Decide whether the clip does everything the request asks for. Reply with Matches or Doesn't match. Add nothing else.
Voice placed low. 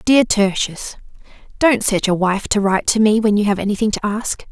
Doesn't match